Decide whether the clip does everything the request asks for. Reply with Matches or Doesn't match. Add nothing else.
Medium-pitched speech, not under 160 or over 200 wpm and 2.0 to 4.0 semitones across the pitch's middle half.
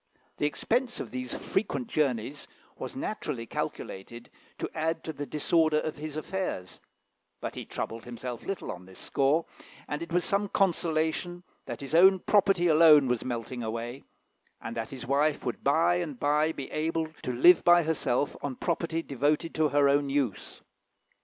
Doesn't match